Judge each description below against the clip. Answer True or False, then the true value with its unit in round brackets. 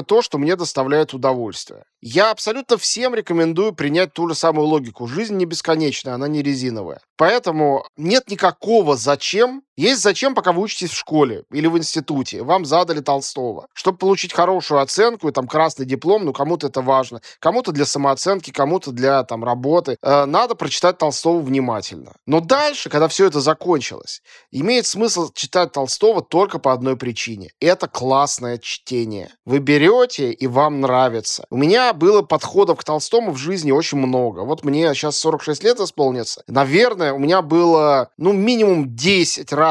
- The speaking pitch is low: False (155 Hz)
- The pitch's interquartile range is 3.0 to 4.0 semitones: False (5.4 semitones)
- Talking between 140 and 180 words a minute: True (160 wpm)